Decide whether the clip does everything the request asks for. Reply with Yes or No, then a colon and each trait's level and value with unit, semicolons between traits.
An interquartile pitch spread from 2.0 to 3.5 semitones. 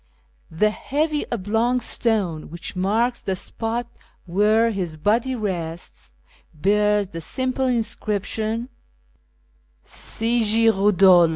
No: average, 4.2 semitones